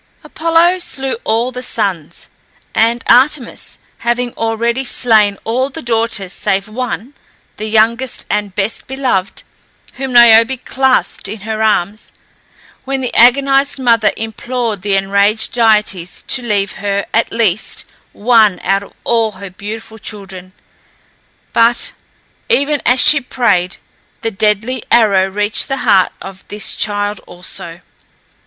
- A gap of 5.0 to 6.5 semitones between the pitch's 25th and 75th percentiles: No, average, 3.6 semitones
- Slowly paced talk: Yes, slow, 130 wpm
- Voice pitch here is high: Yes, high, 225 Hz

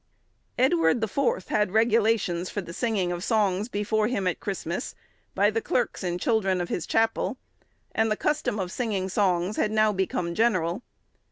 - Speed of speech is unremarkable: Yes, average, 170 wpm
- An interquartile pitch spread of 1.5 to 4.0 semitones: Yes, average, 3.5 semitones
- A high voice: Yes, high, 205 Hz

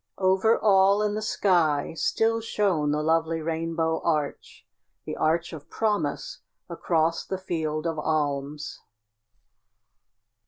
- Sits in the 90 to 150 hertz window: No, medium, 165 Hz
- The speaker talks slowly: Yes, slow, 115 wpm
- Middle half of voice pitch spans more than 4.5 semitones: No, average, 3.9 semitones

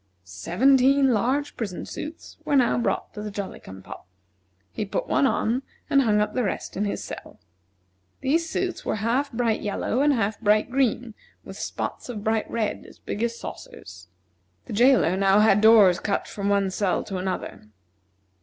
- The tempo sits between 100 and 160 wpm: No, average, 175 wpm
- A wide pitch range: No, average, 4.2 semitones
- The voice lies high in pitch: Yes, high, 220 Hz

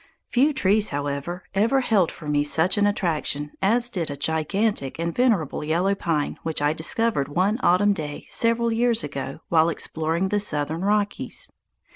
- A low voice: No, medium, 175 Hz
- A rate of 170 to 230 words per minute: No, average, 160 wpm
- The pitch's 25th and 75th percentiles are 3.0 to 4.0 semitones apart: No, wide, 5.6 semitones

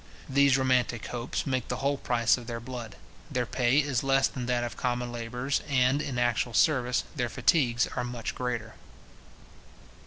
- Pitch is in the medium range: No, low, 125 Hz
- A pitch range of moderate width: No, narrow, 1.7 semitones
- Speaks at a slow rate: No, average, 165 wpm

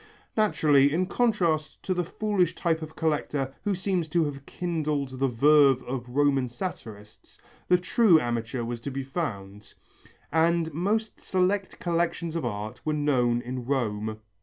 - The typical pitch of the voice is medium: Yes, medium, 150 Hz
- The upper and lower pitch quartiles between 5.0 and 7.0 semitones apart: Yes, wide, 5.6 semitones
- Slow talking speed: No, average, 150 wpm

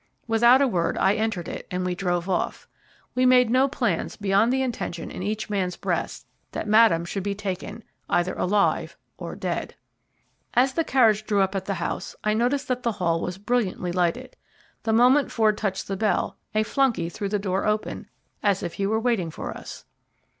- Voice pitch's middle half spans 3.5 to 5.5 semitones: Yes, average, 4.2 semitones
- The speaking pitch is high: Yes, high, 210 Hz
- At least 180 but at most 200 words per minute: Yes, average, 190 wpm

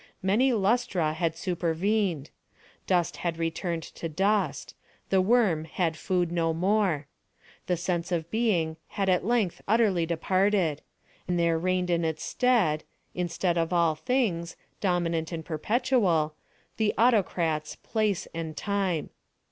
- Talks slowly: Yes, slow, 120 wpm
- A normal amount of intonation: Yes, average, 3.6 semitones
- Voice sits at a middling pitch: Yes, medium, 175 Hz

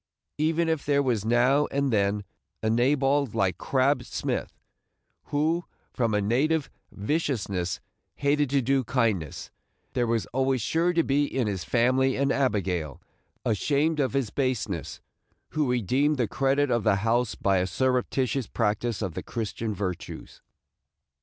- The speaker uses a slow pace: No, average, 145 wpm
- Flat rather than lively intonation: No, average, 4.8 semitones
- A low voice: Yes, low, 125 Hz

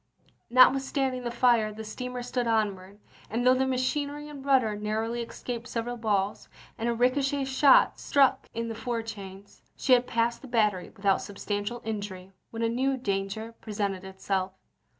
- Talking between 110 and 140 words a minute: No, average, 165 wpm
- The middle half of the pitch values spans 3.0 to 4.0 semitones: Yes, average, 3.6 semitones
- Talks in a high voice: Yes, high, 230 Hz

